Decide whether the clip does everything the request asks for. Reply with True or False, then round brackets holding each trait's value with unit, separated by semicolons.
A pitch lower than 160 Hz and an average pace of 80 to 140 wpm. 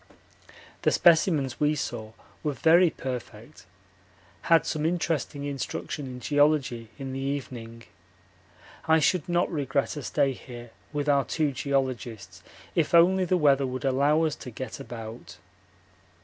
True (140 Hz; 135 wpm)